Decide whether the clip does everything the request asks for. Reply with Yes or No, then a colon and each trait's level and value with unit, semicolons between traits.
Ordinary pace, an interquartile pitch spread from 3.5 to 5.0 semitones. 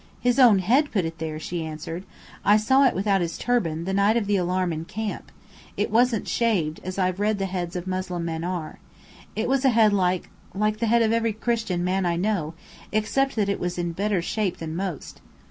No: fast, 215 wpm; average, 4.0 semitones